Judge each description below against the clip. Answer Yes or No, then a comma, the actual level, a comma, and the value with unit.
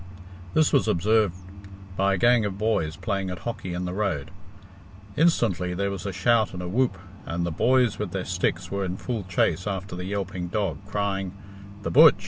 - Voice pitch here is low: Yes, very low, 95 Hz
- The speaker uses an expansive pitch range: No, average, 3.2 semitones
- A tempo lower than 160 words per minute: No, average, 190 wpm